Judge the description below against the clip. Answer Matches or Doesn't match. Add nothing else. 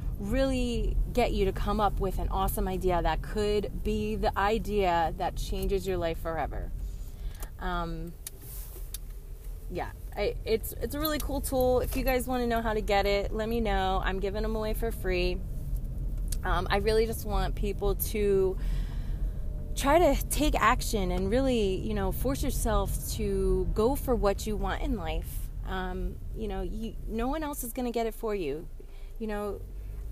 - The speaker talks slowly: Doesn't match